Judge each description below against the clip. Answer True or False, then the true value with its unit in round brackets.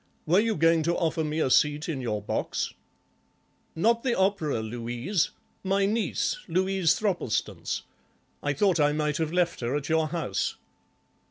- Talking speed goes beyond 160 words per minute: False (150 wpm)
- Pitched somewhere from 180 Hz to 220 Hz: False (160 Hz)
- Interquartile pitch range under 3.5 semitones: False (4.6 semitones)